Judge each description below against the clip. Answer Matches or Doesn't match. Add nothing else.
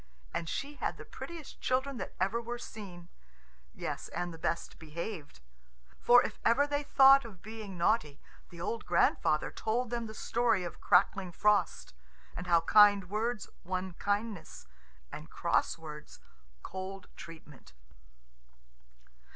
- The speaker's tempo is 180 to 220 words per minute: Doesn't match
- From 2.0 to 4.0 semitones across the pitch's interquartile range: Doesn't match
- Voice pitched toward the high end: Matches